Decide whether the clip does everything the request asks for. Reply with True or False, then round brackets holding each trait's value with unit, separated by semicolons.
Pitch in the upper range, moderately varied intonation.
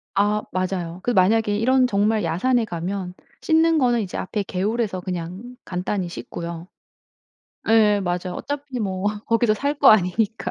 True (205 Hz; 4.4 semitones)